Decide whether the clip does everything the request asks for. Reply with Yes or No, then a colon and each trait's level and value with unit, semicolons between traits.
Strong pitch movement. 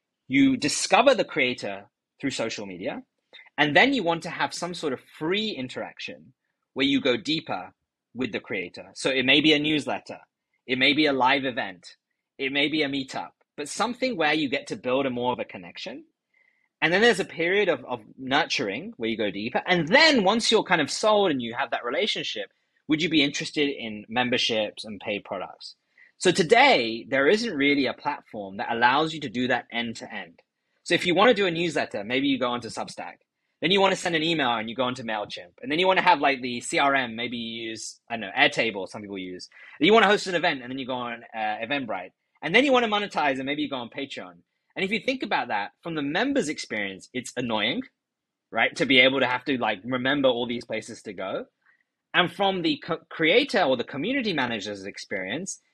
Yes: wide, 6.8 semitones